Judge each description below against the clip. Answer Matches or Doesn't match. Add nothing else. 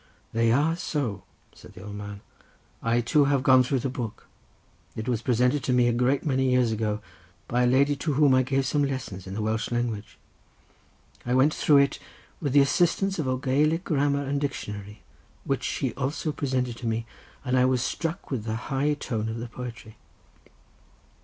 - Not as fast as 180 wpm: Doesn't match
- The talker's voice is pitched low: Matches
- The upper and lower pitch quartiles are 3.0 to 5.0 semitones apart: Matches